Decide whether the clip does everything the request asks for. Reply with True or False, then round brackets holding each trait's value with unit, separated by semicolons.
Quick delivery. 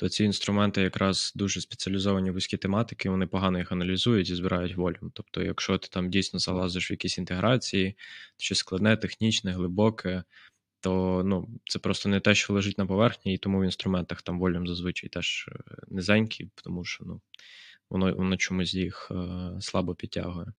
True (165 wpm)